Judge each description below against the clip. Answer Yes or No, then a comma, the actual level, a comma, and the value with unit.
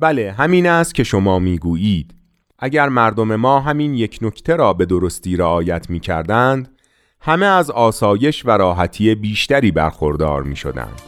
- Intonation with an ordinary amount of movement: No, wide, 7.5 semitones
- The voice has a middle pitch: No, low, 110 Hz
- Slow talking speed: No, average, 135 wpm